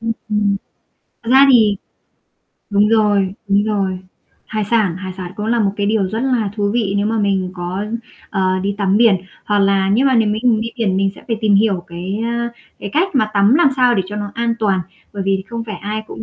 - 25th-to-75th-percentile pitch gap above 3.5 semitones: No, narrow, 2.5 semitones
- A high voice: Yes, high, 210 Hz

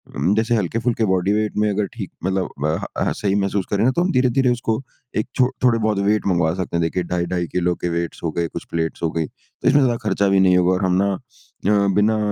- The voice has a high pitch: No, low, 100 Hz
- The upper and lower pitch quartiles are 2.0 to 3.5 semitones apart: No, average, 3.9 semitones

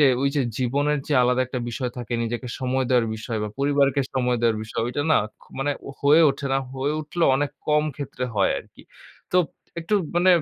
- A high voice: No, low, 135 Hz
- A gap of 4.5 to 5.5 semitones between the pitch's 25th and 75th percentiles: No, average, 2.9 semitones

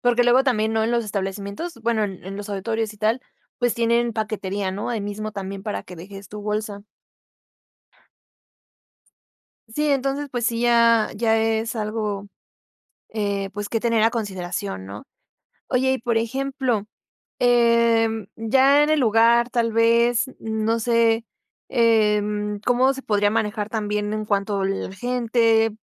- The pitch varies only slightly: Yes, narrow, 2.3 semitones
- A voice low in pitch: No, high, 225 Hz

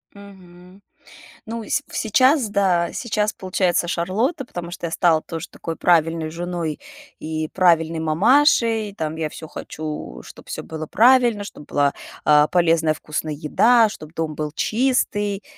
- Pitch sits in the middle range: Yes, medium, 175 Hz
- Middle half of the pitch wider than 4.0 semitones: Yes, average, 4.9 semitones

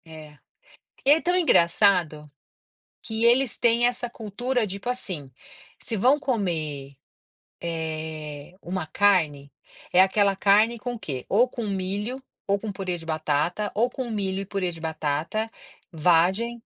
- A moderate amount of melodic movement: No, wide, 6.2 semitones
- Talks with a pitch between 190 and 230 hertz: Yes, high, 195 Hz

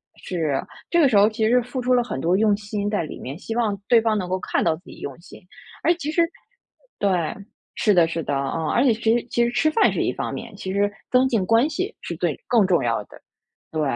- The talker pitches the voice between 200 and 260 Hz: Yes, high, 210 Hz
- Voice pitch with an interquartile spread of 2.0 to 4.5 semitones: No, wide, 5.5 semitones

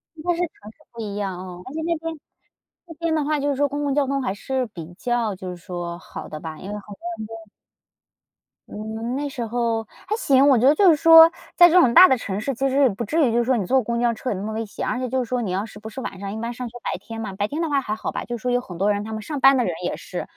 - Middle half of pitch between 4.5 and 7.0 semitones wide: Yes, average, 5.1 semitones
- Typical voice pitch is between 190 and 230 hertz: No, high, 240 Hz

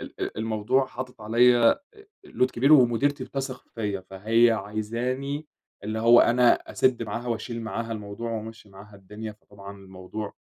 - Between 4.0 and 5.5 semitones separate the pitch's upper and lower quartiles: No, average, 2.9 semitones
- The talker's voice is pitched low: Yes, low, 115 Hz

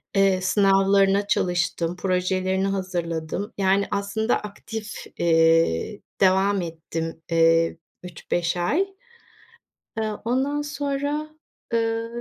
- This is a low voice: No, high, 195 Hz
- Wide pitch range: No, average, 3.9 semitones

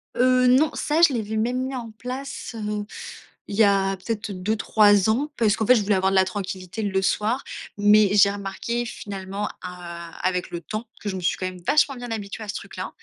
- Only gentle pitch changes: No, average, 3.4 semitones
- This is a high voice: Yes, high, 210 Hz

